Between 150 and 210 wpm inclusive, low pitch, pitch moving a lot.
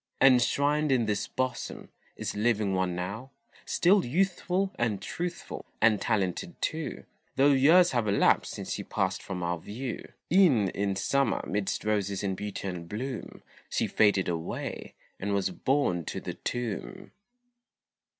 No: average, 140 wpm; low, 110 Hz; wide, 6.1 semitones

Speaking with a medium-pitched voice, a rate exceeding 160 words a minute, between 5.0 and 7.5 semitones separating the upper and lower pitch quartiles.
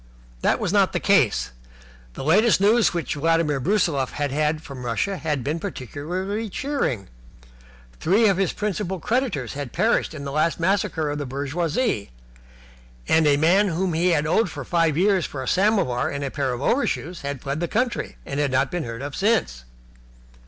Yes: medium, 160 Hz; average, 180 wpm; wide, 5.5 semitones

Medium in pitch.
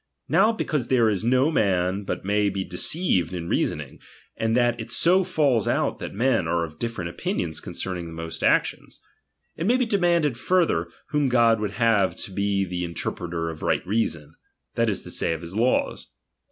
No: low, 105 Hz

